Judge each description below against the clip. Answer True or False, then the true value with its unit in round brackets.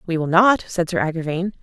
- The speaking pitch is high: False (175 Hz)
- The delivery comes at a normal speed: False (220 wpm)